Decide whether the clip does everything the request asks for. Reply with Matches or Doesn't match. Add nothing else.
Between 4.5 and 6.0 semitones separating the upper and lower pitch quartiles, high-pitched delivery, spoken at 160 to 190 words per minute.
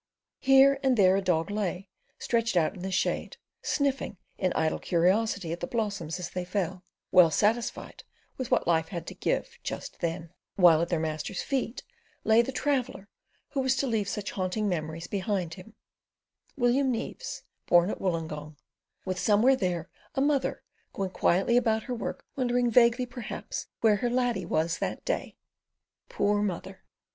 Matches